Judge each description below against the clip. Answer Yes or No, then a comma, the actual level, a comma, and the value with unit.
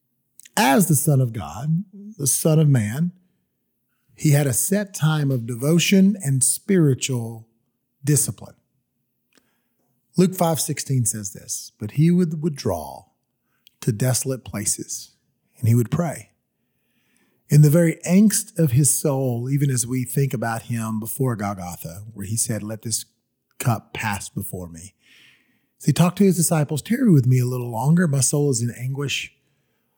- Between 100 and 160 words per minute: Yes, average, 150 wpm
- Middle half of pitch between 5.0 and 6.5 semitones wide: Yes, wide, 5.4 semitones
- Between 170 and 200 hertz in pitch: No, low, 135 Hz